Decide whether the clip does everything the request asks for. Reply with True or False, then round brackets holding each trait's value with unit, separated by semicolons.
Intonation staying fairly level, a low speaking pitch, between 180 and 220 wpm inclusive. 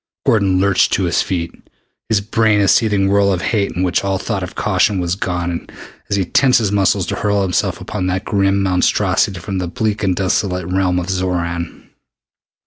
True (1.9 semitones; 95 Hz; 190 wpm)